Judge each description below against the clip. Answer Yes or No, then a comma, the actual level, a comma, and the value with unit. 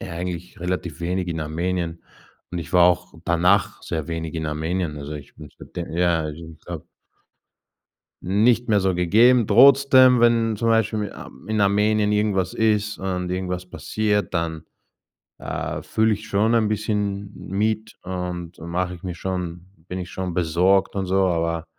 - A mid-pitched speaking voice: No, very low, 90 Hz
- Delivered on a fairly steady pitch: No, average, 3.7 semitones